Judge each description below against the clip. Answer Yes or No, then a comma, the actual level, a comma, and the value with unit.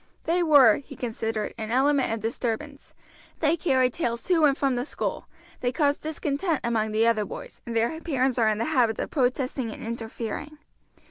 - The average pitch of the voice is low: No, very high, 255 Hz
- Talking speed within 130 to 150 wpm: No, average, 185 wpm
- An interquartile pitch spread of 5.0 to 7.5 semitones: No, average, 4.5 semitones